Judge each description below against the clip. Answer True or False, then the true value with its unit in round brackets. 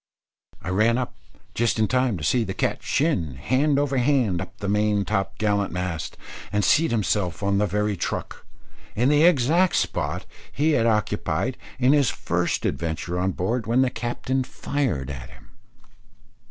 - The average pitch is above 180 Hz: False (110 Hz)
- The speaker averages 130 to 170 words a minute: True (165 wpm)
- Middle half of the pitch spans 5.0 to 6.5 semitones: True (5.6 semitones)